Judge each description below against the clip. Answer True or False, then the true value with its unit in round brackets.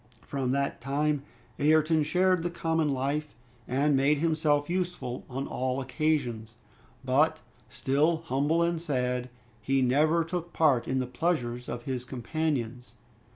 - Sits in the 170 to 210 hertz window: False (145 Hz)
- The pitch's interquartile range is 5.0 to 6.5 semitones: False (3.8 semitones)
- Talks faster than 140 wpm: False (135 wpm)